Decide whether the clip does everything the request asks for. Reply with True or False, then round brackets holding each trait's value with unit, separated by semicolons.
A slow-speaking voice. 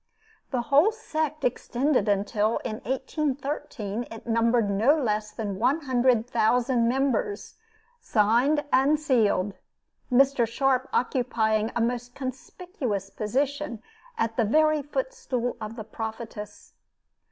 True (115 wpm)